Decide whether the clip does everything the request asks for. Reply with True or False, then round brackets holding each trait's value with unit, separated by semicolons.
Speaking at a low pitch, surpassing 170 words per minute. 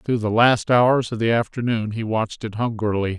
True (115 Hz; 205 wpm)